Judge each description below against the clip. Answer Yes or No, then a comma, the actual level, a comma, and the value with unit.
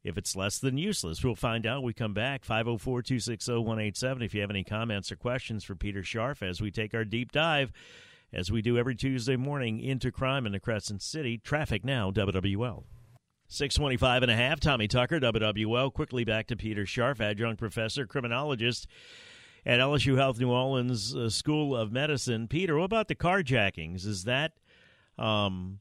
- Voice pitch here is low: Yes, low, 120 Hz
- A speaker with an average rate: Yes, average, 180 wpm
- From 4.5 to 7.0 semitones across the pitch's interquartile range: No, average, 3.6 semitones